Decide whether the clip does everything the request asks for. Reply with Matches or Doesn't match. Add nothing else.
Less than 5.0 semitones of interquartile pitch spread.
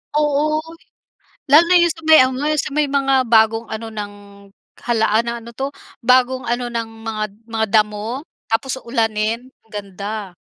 Matches